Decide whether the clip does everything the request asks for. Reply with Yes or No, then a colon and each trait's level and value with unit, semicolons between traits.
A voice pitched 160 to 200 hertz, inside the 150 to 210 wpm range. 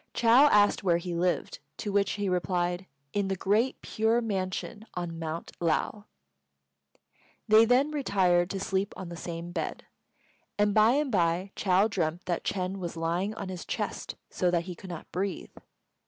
Yes: high, 190 Hz; average, 170 wpm